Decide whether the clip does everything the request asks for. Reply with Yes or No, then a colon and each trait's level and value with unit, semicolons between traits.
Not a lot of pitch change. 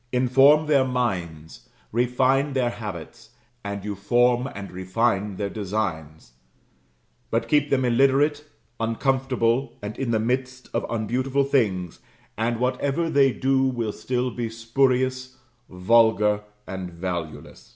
No: average, 4.3 semitones